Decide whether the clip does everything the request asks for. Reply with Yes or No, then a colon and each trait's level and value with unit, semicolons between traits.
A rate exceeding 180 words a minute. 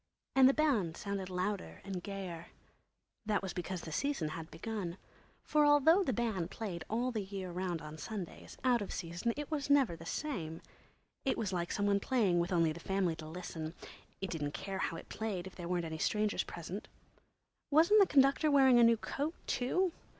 Yes: average, 195 wpm